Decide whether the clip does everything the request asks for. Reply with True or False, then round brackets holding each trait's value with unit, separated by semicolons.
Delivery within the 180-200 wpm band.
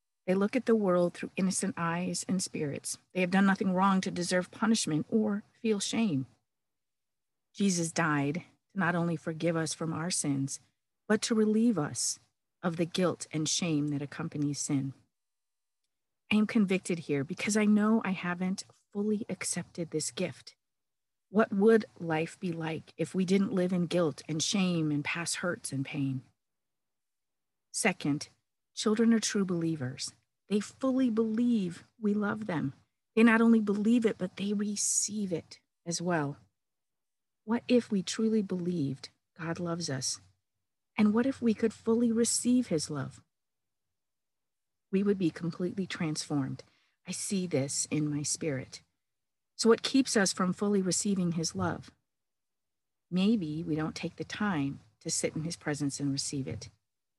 False (155 wpm)